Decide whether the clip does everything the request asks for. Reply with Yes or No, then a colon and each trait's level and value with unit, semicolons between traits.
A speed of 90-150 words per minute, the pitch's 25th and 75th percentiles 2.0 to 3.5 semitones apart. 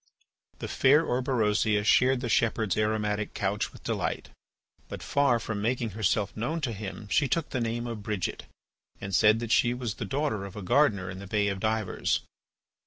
No: average, 180 wpm; average, 3.0 semitones